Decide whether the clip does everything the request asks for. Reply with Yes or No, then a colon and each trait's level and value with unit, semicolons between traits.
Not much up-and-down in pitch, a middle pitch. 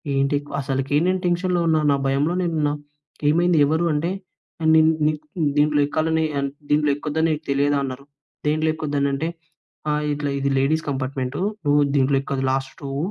Yes: narrow, 2.3 semitones; medium, 145 Hz